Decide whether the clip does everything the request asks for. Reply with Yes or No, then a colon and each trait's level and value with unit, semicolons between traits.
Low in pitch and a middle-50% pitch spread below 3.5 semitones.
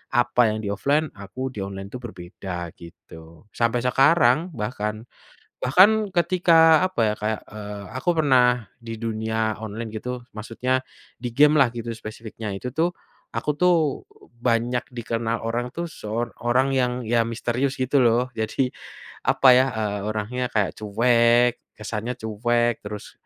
Yes: low, 120 Hz; average, 3.0 semitones